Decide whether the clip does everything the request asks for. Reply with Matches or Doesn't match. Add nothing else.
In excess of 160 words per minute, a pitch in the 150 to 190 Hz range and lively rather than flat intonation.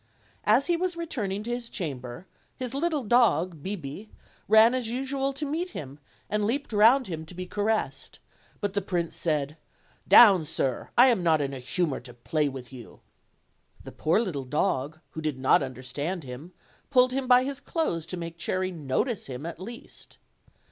Matches